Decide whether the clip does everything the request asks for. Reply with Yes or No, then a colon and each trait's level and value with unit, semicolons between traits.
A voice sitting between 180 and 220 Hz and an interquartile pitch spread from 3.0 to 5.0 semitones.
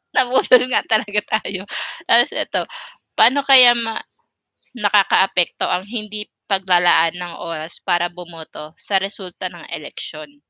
Yes: high, 190 Hz; average, 3.6 semitones